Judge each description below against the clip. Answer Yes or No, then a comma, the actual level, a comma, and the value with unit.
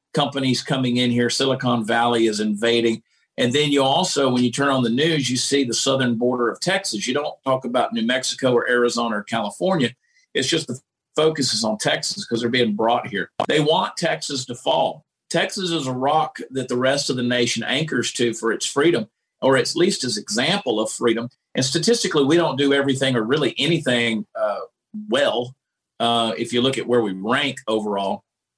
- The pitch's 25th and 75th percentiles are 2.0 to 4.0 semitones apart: Yes, average, 3.2 semitones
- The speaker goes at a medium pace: Yes, average, 195 wpm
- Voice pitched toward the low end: Yes, low, 125 Hz